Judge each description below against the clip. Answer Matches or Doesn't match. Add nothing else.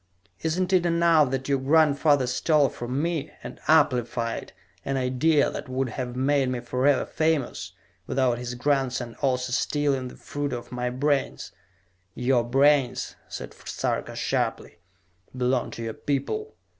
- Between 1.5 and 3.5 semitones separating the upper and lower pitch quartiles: Matches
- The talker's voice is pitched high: Doesn't match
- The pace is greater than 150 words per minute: Doesn't match